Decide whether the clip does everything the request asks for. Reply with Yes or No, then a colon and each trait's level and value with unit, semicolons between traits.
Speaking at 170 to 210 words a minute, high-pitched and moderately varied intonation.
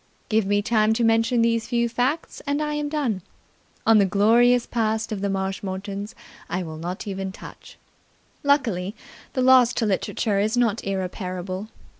No: average, 160 wpm; high, 220 Hz; average, 3.7 semitones